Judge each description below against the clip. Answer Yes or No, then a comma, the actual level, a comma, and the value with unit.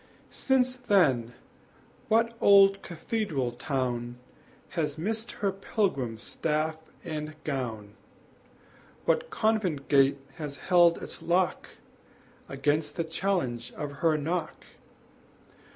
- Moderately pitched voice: Yes, medium, 160 Hz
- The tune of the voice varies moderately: No, wide, 6.2 semitones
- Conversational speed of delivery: No, slow, 100 wpm